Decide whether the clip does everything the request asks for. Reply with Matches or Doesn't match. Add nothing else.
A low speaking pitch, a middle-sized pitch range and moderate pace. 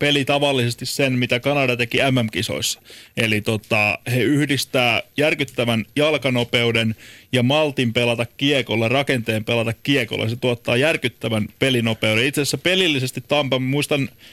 Matches